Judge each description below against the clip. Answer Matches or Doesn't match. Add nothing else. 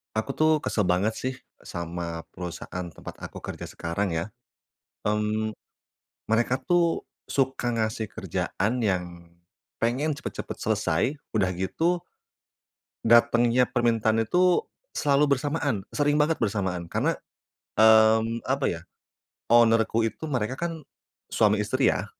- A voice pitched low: Matches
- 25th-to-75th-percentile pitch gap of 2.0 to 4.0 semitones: Doesn't match